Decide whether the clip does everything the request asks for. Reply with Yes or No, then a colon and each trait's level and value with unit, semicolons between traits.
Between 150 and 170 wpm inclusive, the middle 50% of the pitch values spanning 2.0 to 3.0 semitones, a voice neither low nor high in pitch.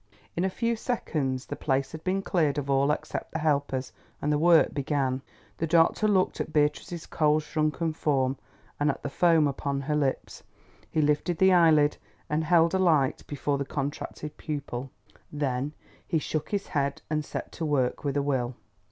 No: average, 180 wpm; average, 2.7 semitones; medium, 150 Hz